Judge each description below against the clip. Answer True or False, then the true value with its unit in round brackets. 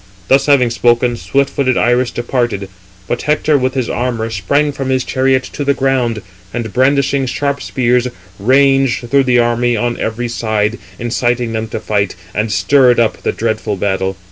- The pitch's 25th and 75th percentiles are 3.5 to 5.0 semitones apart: False (2.8 semitones)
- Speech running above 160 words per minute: True (170 wpm)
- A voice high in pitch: False (120 Hz)